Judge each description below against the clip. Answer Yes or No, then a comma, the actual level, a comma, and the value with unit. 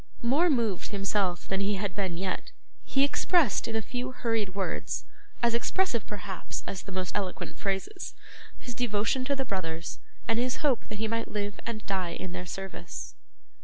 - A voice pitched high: Yes, high, 210 Hz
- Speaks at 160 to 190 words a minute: Yes, average, 175 wpm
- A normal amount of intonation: Yes, average, 4.2 semitones